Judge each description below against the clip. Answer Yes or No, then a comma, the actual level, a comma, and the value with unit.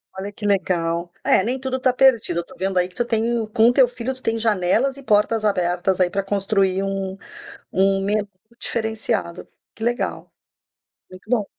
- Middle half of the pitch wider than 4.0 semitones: No, average, 3.6 semitones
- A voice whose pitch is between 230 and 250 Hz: No, high, 205 Hz